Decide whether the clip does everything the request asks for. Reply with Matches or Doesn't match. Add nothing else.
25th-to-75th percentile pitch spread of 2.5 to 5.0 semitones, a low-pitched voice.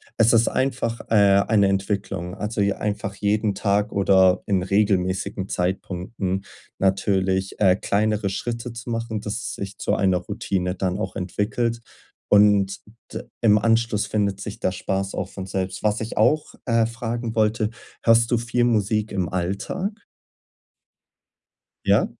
Matches